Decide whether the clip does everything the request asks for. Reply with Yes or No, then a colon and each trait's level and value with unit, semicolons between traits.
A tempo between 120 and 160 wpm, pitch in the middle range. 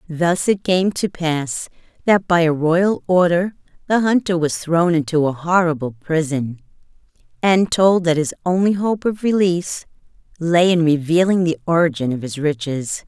Yes: average, 155 wpm; medium, 170 Hz